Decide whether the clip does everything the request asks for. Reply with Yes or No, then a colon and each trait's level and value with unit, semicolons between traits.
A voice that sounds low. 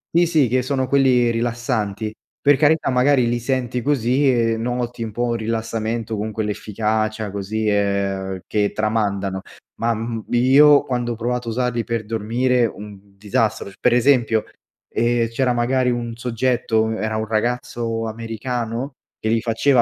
Yes: low, 115 Hz